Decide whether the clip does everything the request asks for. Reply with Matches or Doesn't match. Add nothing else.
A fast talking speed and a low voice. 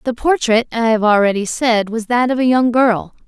Doesn't match